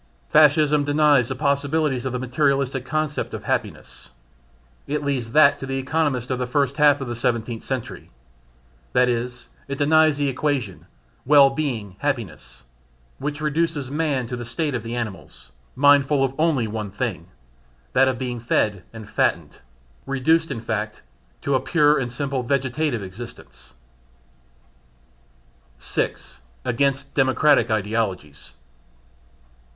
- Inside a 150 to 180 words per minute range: No, slow, 135 wpm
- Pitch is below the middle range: Yes, low, 130 Hz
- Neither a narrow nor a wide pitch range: Yes, average, 3.6 semitones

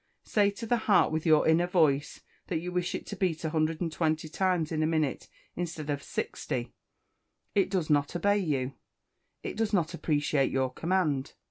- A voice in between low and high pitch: Yes, medium, 160 Hz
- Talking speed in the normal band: Yes, average, 170 wpm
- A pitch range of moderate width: Yes, average, 3.0 semitones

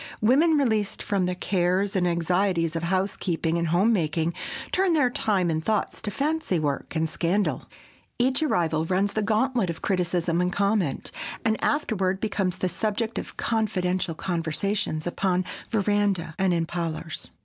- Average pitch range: Yes, average, 4.0 semitones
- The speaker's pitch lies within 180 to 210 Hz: Yes, medium, 185 Hz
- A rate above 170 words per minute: No, average, 150 wpm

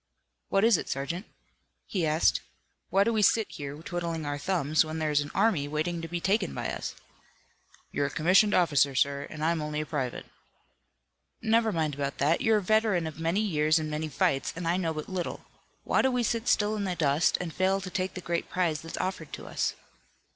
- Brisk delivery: Yes, fast, 210 wpm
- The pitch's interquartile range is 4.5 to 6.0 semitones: No, average, 4.0 semitones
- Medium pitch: Yes, medium, 165 Hz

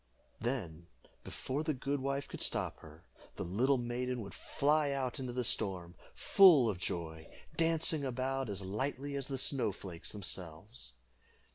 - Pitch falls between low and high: No, low, 125 Hz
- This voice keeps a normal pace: Yes, average, 150 wpm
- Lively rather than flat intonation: Yes, wide, 6.7 semitones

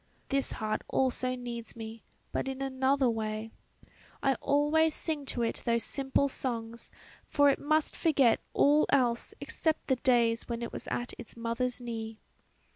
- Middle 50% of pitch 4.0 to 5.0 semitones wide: No, average, 3.0 semitones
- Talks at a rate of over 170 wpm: No, average, 155 wpm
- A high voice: Yes, very high, 250 Hz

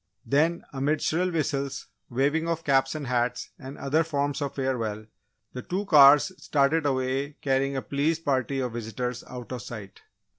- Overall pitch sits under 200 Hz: Yes, medium, 140 Hz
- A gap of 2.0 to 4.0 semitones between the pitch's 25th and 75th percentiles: Yes, average, 2.9 semitones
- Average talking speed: Yes, average, 160 wpm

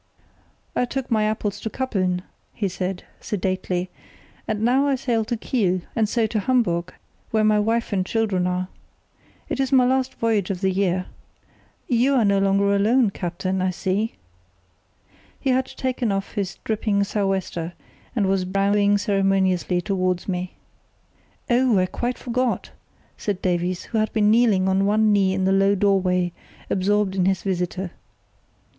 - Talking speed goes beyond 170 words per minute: No, average, 160 wpm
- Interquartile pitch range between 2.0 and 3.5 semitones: Yes, average, 3.2 semitones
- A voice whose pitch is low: No, high, 200 Hz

